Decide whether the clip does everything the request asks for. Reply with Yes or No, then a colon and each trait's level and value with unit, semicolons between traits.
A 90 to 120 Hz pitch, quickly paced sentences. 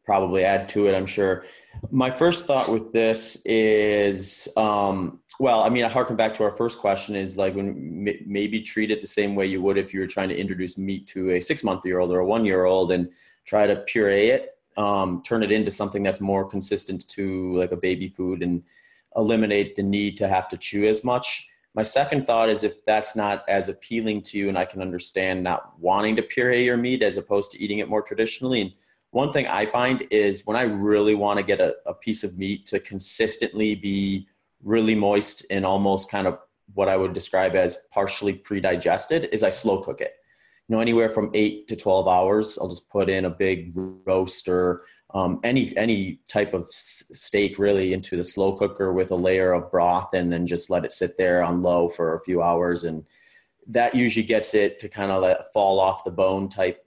Yes: low, 100 Hz; fast, 215 wpm